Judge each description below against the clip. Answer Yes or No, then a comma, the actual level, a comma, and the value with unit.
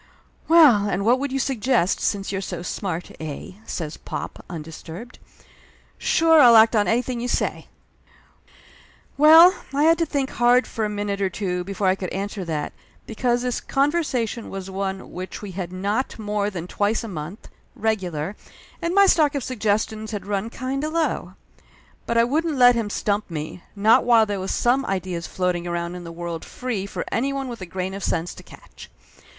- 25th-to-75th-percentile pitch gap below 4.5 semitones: No, average, 5.2 semitones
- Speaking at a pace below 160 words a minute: No, average, 190 wpm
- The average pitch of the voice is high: Yes, high, 210 Hz